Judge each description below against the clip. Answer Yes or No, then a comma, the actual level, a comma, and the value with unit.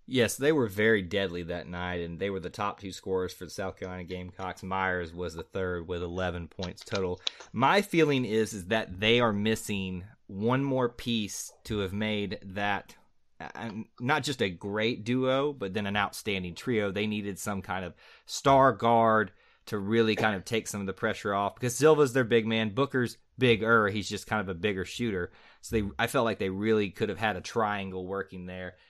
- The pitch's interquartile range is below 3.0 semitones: No, average, 3.6 semitones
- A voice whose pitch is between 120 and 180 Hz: No, low, 105 Hz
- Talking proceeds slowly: No, average, 200 wpm